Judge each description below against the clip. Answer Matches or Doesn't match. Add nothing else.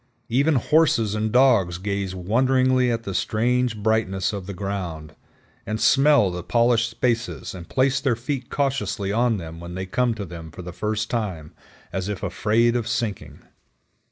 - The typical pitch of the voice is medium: Doesn't match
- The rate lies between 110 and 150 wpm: Doesn't match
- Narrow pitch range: Doesn't match